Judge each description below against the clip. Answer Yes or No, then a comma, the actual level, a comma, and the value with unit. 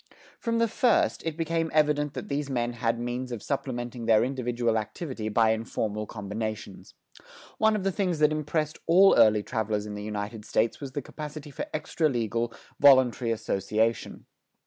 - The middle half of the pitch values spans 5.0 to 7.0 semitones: Yes, wide, 5.4 semitones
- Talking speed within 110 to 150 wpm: No, average, 165 wpm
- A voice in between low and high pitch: No, low, 120 Hz